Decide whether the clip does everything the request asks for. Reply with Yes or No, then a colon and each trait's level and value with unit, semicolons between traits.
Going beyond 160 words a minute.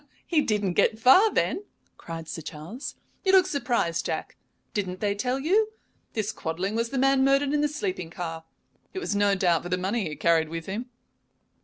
Yes: average, 190 wpm